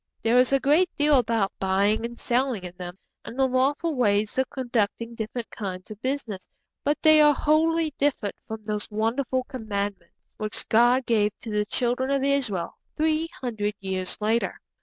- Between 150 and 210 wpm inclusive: Yes, average, 170 wpm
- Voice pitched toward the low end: No, high, 235 Hz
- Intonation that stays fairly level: No, average, 4.6 semitones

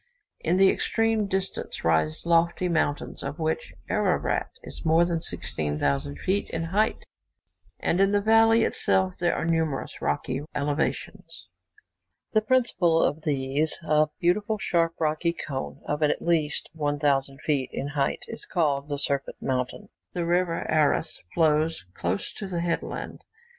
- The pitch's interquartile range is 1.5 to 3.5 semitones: No, average, 3.9 semitones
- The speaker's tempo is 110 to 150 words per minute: Yes, average, 140 wpm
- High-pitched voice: No, medium, 160 Hz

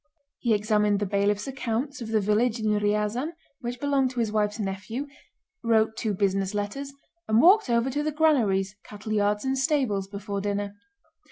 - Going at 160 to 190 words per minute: Yes, average, 170 wpm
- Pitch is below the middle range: No, high, 215 Hz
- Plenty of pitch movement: No, average, 3.8 semitones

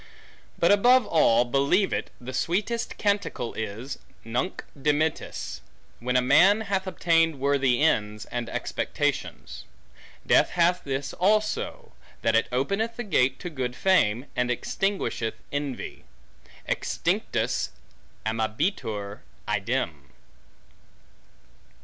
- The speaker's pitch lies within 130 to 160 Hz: Yes, medium, 140 Hz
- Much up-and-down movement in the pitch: Yes, wide, 7.7 semitones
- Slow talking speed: Yes, slow, 105 wpm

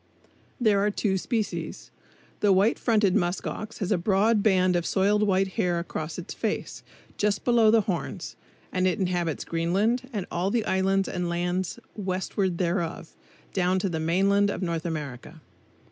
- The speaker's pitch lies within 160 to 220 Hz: Yes, high, 190 Hz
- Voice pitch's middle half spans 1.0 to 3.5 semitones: Yes, average, 2.9 semitones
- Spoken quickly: No, average, 160 wpm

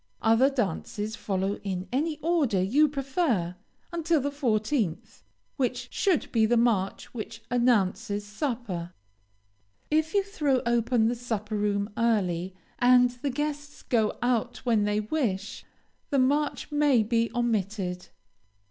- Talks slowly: Yes, slow, 130 wpm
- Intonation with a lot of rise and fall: No, average, 5.0 semitones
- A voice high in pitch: Yes, high, 235 Hz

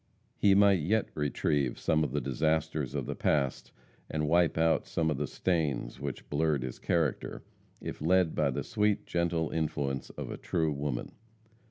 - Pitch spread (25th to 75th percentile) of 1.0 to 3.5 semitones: Yes, average, 2.8 semitones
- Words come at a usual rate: Yes, average, 170 wpm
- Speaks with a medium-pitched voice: No, very low, 80 Hz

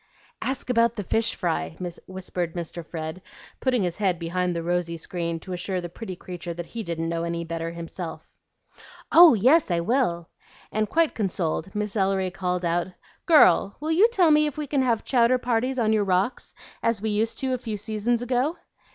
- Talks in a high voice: Yes, high, 195 Hz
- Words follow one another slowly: No, average, 190 wpm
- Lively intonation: Yes, wide, 5.9 semitones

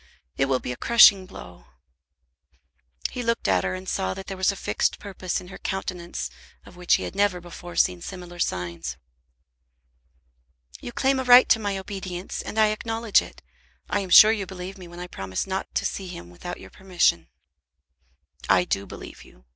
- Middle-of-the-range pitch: Yes, medium, 180 Hz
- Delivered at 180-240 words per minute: Yes, average, 185 wpm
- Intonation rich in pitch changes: Yes, wide, 8.4 semitones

